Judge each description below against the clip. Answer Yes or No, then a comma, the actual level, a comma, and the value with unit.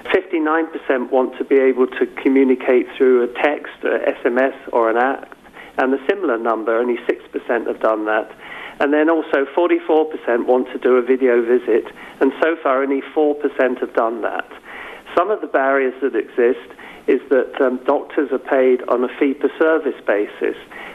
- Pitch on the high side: No, low, 135 Hz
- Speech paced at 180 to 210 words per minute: No, average, 165 wpm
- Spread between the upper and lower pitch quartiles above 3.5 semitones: Yes, average, 4.3 semitones